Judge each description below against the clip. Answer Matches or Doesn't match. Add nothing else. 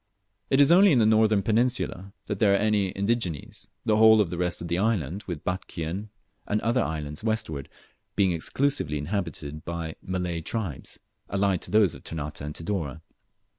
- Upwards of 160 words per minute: Matches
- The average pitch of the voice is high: Doesn't match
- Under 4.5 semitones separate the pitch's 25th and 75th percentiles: Doesn't match